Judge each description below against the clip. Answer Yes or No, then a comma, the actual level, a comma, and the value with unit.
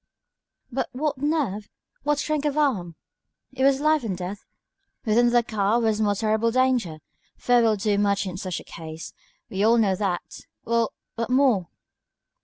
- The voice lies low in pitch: No, high, 225 Hz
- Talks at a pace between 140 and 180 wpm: Yes, average, 165 wpm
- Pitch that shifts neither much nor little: Yes, average, 4.7 semitones